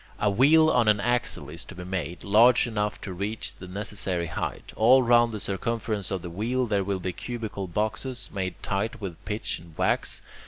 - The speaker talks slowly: No, average, 195 wpm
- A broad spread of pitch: No, average, 3.7 semitones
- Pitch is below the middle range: Yes, low, 105 Hz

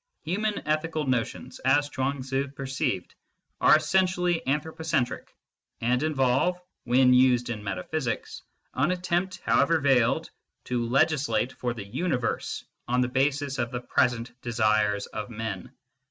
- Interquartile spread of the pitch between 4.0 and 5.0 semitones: Yes, average, 4.4 semitones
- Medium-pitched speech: No, low, 130 Hz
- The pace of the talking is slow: Yes, slow, 130 wpm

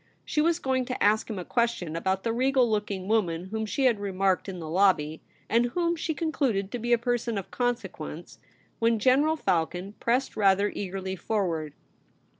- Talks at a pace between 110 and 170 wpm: No, average, 180 wpm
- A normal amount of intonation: Yes, average, 4.5 semitones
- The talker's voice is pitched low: No, high, 215 Hz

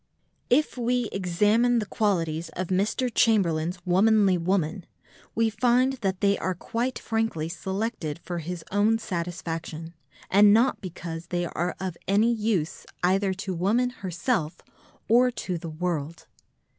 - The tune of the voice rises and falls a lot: No, average, 4.7 semitones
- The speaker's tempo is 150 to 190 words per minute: No, slow, 135 wpm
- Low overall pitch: No, high, 190 Hz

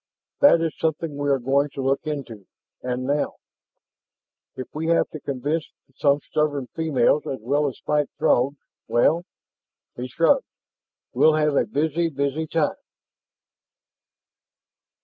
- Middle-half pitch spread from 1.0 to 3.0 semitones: Yes, average, 2.7 semitones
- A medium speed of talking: No, slow, 130 wpm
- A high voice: No, medium, 145 Hz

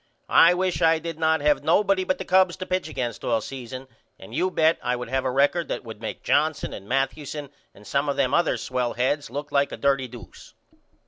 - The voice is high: No, medium, 140 Hz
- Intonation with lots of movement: No, average, 4.4 semitones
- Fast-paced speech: Yes, fast, 220 wpm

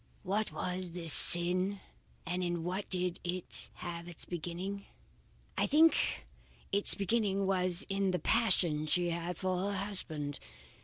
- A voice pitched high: No, medium, 180 Hz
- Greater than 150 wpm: No, average, 140 wpm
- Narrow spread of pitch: Yes, narrow, 2.3 semitones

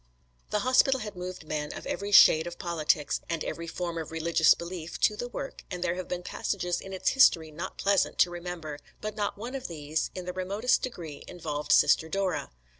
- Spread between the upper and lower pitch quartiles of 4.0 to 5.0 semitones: No, average, 3.6 semitones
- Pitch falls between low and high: Yes, medium, 175 Hz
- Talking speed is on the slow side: No, average, 200 wpm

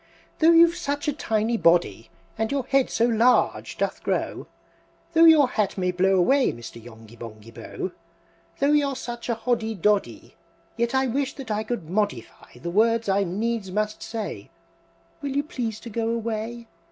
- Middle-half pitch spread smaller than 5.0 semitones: No, wide, 5.4 semitones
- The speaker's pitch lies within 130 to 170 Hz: No, high, 225 Hz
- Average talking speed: Yes, average, 175 wpm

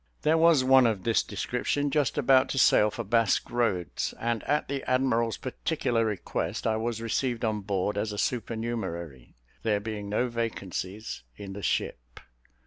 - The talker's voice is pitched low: Yes, low, 115 Hz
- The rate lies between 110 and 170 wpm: Yes, average, 160 wpm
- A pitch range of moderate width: Yes, average, 3.8 semitones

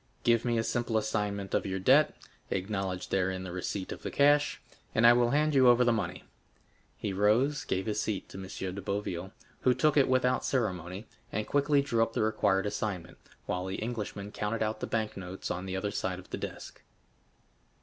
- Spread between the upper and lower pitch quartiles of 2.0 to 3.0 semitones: No, average, 4.1 semitones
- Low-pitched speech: Yes, low, 105 Hz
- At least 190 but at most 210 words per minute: Yes, average, 200 wpm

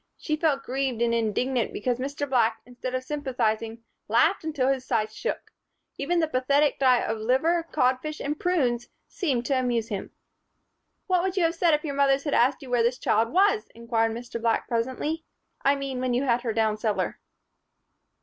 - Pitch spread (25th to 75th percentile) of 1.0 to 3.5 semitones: No, average, 4.0 semitones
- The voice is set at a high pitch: Yes, very high, 255 Hz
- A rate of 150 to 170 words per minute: No, average, 185 wpm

